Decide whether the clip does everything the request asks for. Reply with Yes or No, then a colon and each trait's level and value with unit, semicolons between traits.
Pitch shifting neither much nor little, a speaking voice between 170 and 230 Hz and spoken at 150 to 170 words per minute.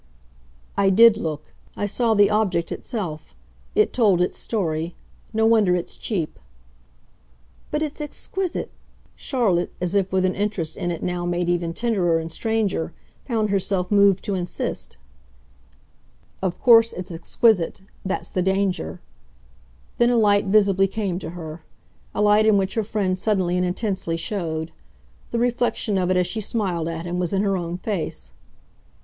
Yes: average, 3.6 semitones; high, 190 Hz; average, 155 wpm